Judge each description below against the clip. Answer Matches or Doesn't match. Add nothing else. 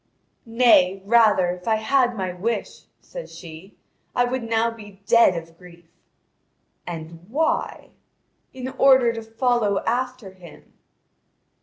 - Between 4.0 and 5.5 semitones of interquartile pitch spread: Matches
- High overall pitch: Matches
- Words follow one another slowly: Matches